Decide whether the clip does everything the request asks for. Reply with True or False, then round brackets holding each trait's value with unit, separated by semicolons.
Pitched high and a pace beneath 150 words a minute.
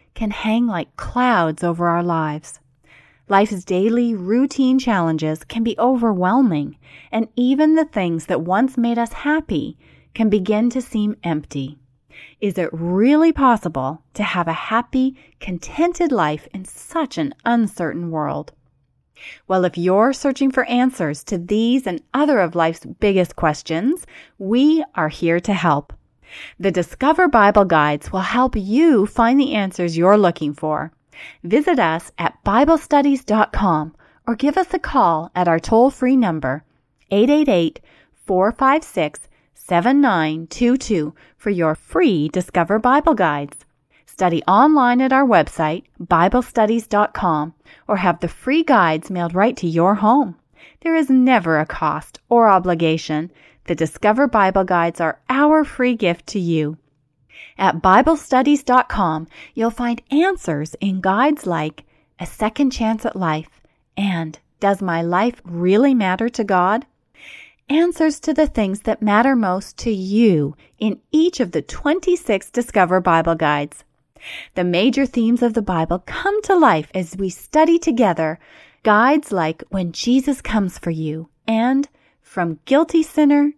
True (205 Hz; 140 wpm)